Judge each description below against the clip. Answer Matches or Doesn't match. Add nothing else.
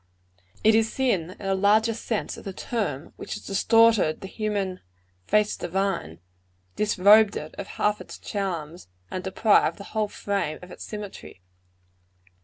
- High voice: Matches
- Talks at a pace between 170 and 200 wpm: Doesn't match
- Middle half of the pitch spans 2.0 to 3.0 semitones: Matches